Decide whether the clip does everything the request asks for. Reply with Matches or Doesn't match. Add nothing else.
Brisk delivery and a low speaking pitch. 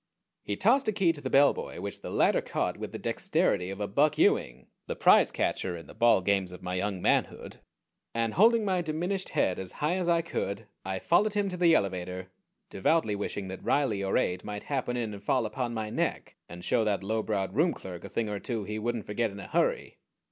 Matches